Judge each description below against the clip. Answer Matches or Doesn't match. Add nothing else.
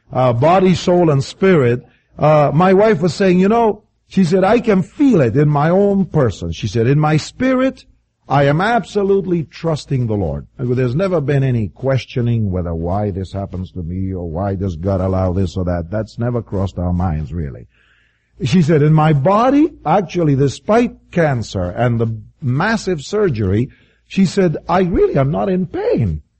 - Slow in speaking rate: Doesn't match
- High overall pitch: Doesn't match